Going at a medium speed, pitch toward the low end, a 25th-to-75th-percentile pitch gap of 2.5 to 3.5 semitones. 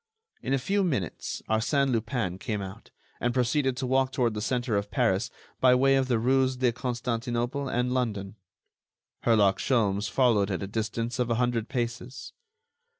Yes: average, 165 wpm; low, 120 Hz; average, 2.9 semitones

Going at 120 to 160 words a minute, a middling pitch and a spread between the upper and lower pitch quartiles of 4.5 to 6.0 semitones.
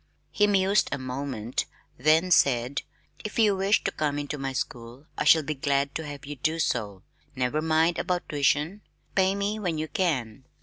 No: average, 180 wpm; medium, 150 Hz; average, 5.0 semitones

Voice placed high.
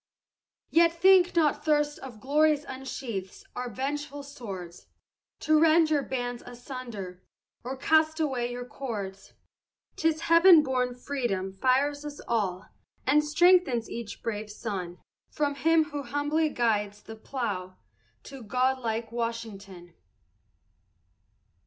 Yes: very high, 260 Hz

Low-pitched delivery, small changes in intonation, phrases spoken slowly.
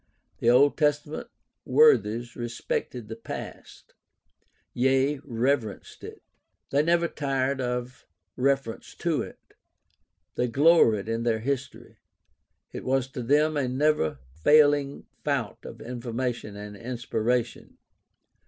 No: low, 125 Hz; average, 3.4 semitones; slow, 110 wpm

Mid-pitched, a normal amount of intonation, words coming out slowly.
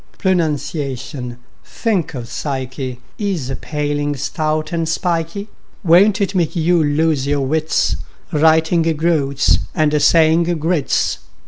Yes: medium, 155 Hz; average, 3.0 semitones; slow, 110 wpm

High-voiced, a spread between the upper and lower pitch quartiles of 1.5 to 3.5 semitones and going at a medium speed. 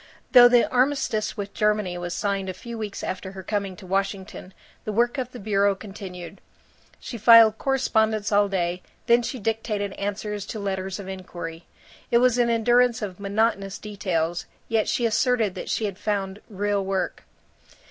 Yes: high, 205 Hz; average, 2.8 semitones; average, 170 wpm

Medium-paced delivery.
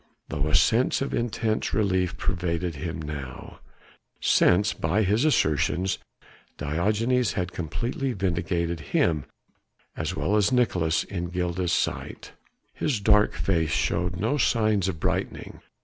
No: slow, 125 wpm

